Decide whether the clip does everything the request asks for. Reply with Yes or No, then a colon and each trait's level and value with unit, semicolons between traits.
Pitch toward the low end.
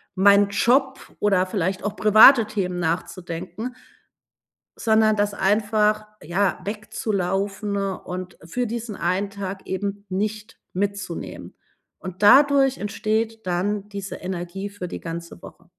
No: high, 200 Hz